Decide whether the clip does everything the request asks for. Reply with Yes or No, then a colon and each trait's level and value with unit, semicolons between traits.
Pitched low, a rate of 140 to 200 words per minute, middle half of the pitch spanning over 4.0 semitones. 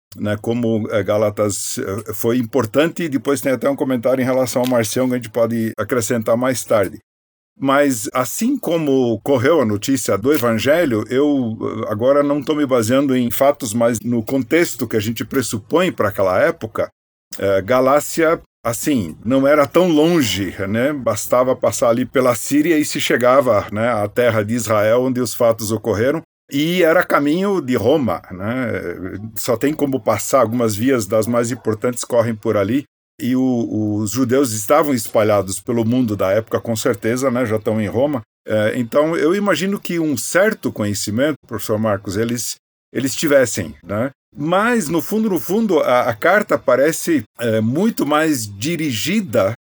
Yes: low, 125 Hz; average, 160 wpm; average, 4.7 semitones